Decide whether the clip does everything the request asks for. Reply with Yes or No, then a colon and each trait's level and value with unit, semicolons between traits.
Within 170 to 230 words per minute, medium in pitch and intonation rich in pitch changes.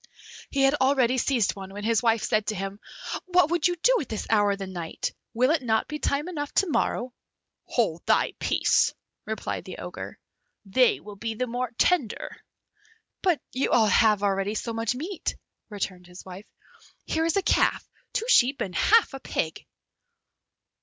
No: average, 175 wpm; high, 235 Hz; wide, 6.1 semitones